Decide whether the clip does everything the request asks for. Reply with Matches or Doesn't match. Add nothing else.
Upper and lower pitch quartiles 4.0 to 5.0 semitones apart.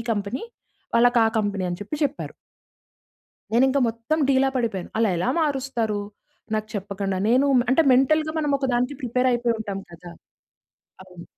Matches